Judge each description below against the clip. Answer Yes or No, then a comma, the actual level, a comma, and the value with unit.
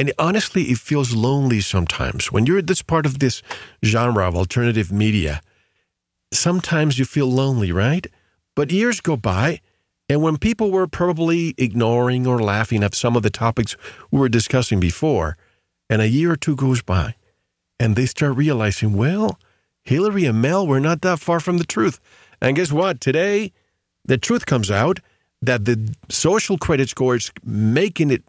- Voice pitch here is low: Yes, low, 130 Hz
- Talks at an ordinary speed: Yes, average, 170 wpm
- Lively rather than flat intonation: Yes, wide, 7.0 semitones